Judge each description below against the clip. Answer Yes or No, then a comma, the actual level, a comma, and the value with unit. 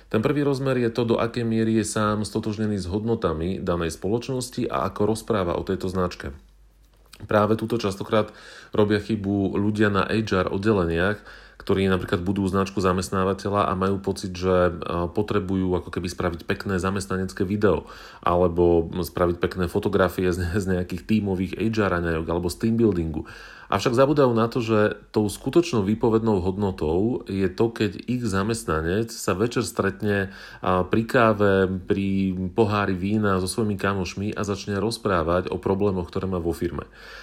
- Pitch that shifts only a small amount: No, average, 3.0 semitones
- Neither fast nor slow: Yes, average, 145 wpm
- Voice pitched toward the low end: Yes, low, 100 Hz